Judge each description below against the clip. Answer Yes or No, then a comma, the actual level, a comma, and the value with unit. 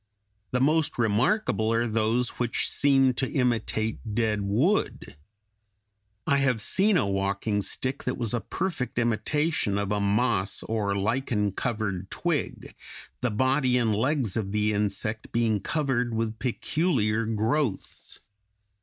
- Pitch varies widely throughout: No, average, 3.8 semitones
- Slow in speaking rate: Yes, slow, 130 wpm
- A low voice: Yes, low, 115 Hz